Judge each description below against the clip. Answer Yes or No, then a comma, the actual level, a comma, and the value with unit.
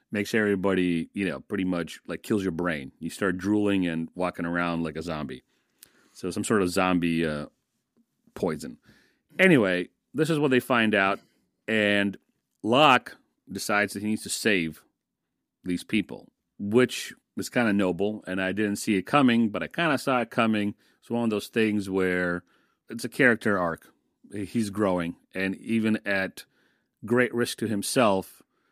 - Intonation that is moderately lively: Yes, average, 3.5 semitones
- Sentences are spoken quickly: No, average, 165 wpm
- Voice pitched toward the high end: No, low, 100 Hz